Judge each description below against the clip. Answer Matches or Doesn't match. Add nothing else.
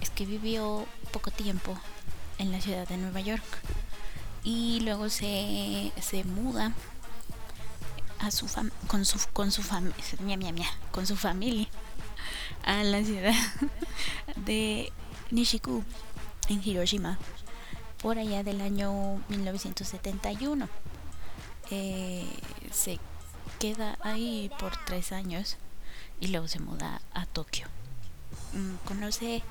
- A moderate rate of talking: Doesn't match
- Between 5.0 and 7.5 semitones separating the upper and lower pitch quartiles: Doesn't match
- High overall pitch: Matches